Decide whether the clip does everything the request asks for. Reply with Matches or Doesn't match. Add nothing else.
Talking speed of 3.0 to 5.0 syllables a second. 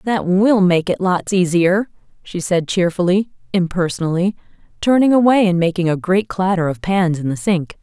Matches